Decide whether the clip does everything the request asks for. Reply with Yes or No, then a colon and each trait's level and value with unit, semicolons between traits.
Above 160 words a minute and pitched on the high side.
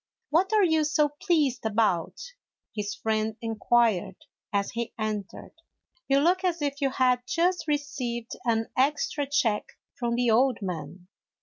No: average, 150 wpm; high, 245 Hz